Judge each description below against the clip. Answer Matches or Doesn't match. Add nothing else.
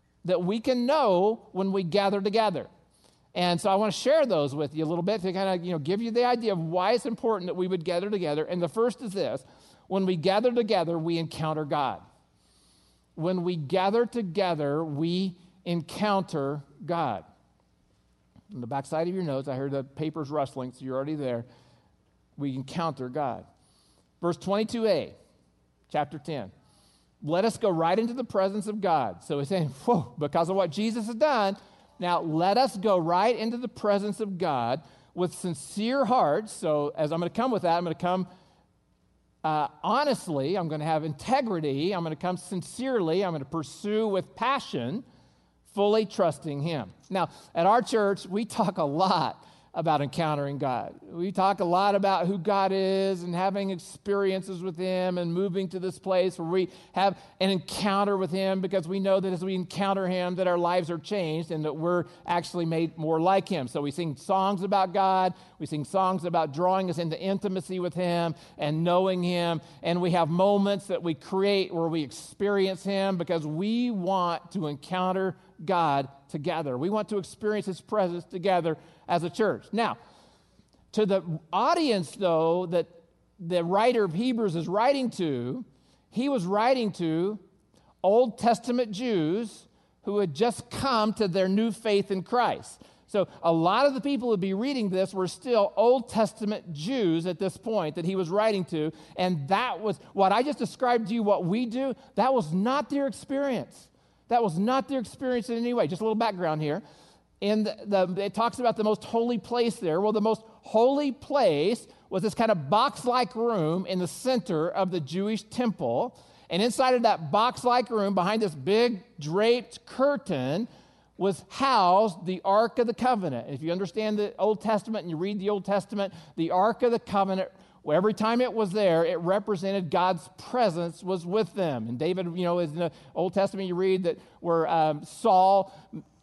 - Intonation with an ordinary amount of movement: Matches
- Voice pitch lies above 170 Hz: Matches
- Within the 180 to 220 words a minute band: Matches